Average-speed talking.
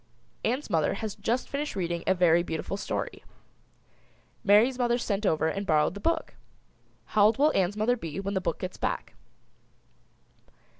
Yes: average, 160 wpm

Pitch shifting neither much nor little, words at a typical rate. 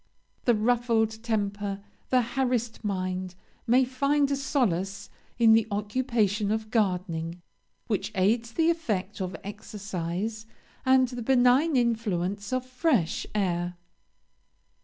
No: average, 4.0 semitones; slow, 115 wpm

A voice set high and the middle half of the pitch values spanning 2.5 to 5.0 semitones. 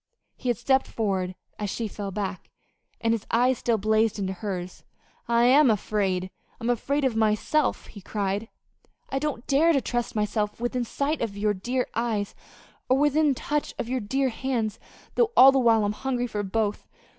Yes: high, 230 Hz; average, 3.9 semitones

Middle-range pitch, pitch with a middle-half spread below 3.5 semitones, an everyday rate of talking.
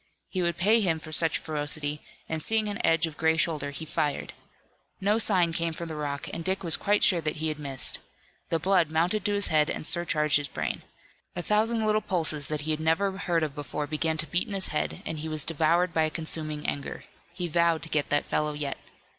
No: medium, 160 Hz; average, 2.8 semitones; fast, 230 wpm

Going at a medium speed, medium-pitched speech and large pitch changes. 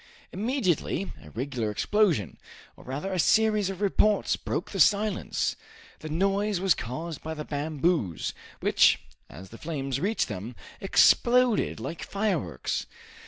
No: slow, 130 wpm; medium, 170 Hz; wide, 7.1 semitones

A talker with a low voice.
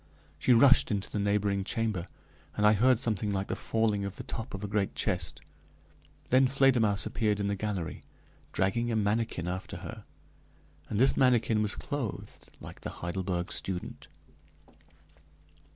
Yes: low, 105 Hz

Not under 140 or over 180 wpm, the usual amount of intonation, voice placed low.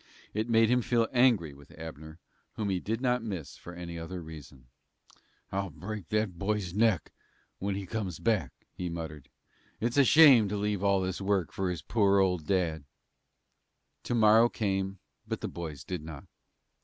Yes: average, 170 wpm; average, 4.4 semitones; very low, 95 Hz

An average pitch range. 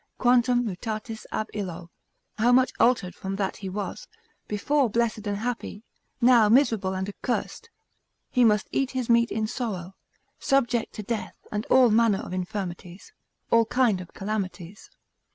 Yes: average, 3.8 semitones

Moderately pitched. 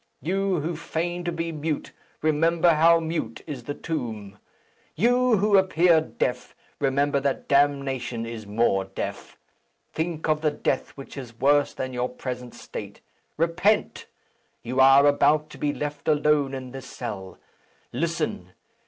Yes: medium, 145 Hz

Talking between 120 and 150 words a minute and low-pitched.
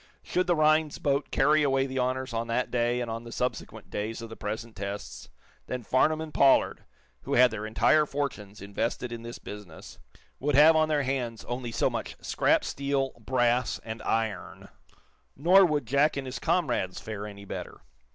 No: average, 180 wpm; low, 125 Hz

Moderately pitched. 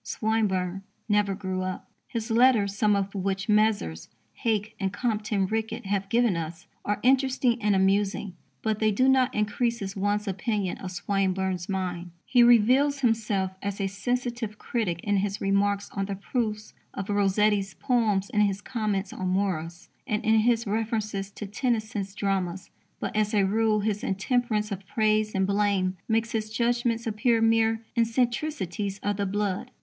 No: high, 210 Hz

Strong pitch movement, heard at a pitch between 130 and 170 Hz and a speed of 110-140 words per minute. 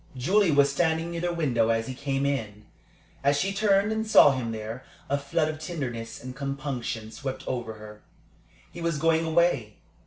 No: wide, 5.7 semitones; medium, 140 Hz; average, 180 wpm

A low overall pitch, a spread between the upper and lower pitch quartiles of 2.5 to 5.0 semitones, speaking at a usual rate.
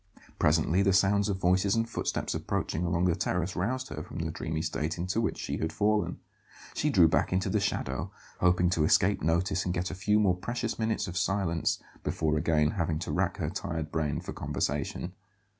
Yes: very low, 90 Hz; average, 3.5 semitones; average, 195 wpm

